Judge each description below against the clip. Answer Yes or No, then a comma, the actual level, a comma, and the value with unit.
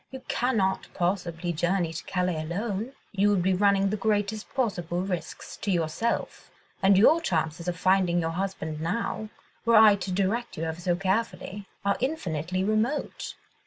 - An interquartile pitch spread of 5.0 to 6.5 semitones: No, average, 3.4 semitones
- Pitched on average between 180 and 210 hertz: Yes, high, 190 Hz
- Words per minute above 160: No, average, 150 wpm